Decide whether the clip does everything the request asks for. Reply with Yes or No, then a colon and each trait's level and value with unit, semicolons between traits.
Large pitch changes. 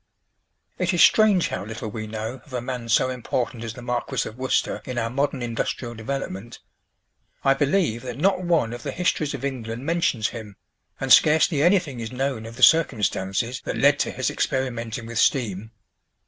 No: average, 3.5 semitones